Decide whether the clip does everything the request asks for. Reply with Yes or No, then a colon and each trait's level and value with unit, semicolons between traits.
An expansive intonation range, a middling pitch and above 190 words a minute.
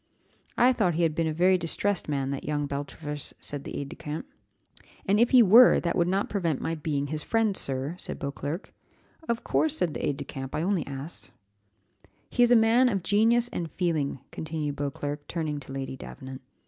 Yes: wide, 5.8 semitones; medium, 160 Hz; average, 200 wpm